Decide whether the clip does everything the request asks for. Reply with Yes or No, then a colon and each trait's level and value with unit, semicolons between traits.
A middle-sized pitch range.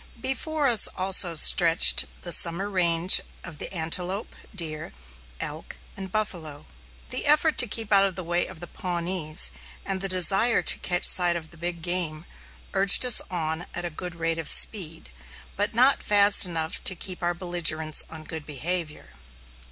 Yes: average, 3.0 semitones